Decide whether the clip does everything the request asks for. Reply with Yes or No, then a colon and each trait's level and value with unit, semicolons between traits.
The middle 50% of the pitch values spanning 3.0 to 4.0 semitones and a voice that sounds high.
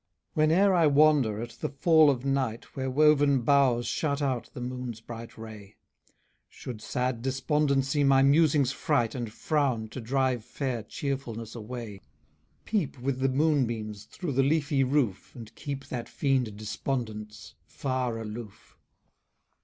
No: average, 3.6 semitones; low, 130 Hz